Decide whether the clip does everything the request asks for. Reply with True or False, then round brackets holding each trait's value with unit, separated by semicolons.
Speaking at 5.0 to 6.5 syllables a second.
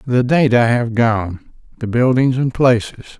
False (4.6 syllables/s)